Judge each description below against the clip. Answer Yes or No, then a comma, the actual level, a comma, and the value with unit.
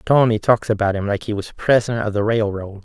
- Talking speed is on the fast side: Yes, fast, 230 wpm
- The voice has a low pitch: Yes, low, 110 Hz